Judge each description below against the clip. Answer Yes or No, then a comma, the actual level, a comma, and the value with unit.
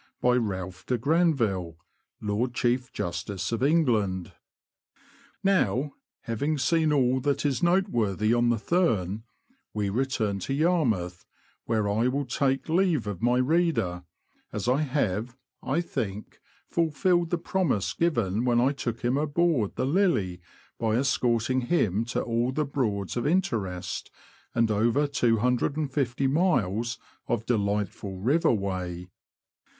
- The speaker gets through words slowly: Yes, slow, 130 wpm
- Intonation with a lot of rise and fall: Yes, wide, 5.8 semitones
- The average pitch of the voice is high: No, low, 120 Hz